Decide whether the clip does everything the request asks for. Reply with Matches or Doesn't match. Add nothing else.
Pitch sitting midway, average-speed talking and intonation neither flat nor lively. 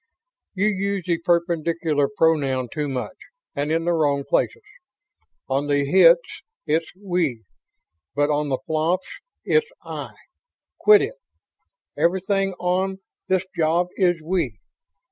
Doesn't match